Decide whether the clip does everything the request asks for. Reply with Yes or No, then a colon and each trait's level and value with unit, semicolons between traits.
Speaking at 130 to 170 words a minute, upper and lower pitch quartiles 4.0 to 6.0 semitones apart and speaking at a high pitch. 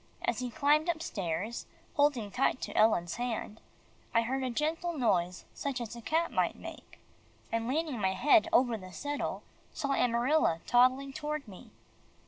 Yes: average, 155 wpm; average, 4.7 semitones; very high, 250 Hz